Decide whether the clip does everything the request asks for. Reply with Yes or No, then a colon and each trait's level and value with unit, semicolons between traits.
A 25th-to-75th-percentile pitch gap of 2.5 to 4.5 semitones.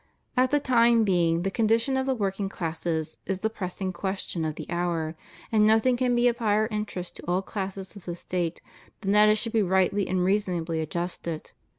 Yes: average, 4.0 semitones